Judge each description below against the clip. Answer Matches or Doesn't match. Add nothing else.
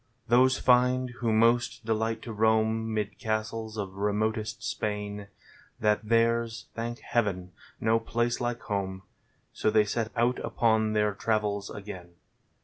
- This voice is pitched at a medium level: Doesn't match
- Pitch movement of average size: Doesn't match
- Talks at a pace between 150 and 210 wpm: Doesn't match